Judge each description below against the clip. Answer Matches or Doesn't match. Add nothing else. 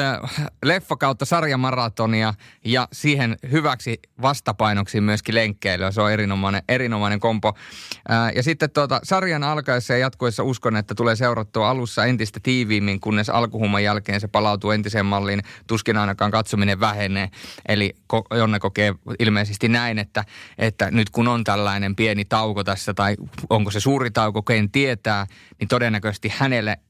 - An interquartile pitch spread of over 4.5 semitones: Doesn't match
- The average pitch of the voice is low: Matches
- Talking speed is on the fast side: Doesn't match